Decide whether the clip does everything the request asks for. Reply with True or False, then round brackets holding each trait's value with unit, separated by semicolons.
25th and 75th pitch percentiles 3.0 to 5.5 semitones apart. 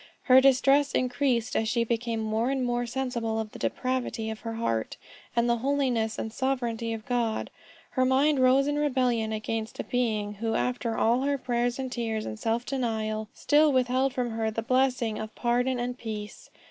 False (2.6 semitones)